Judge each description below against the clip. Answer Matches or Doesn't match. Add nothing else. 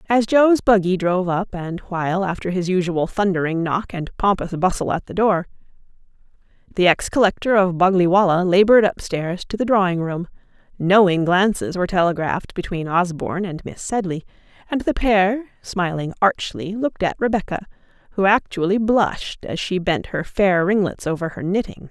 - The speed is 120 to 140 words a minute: Doesn't match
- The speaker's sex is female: Matches